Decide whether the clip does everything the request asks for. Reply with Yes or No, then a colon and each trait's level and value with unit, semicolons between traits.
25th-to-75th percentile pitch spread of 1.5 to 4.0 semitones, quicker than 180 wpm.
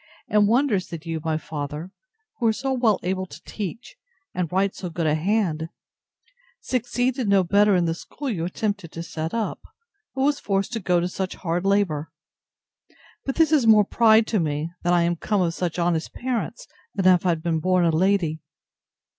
No: average, 4.6 semitones; average, 195 wpm